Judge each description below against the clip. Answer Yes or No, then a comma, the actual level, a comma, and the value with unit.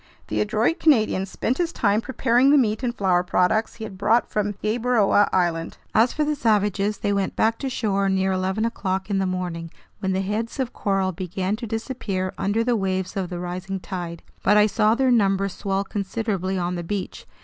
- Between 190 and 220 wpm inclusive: Yes, average, 200 wpm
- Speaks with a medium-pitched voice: No, high, 200 Hz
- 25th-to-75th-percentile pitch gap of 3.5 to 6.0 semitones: No, average, 3.1 semitones